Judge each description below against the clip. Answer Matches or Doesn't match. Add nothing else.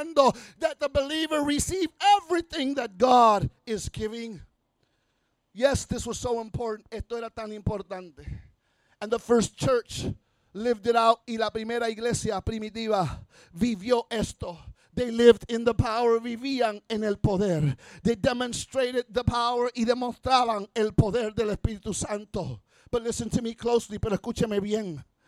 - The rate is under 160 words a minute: Matches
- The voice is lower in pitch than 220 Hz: Doesn't match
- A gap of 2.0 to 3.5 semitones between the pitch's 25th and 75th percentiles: Matches